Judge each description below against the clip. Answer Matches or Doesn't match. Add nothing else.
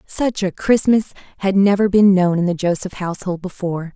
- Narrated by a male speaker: Doesn't match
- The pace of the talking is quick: Doesn't match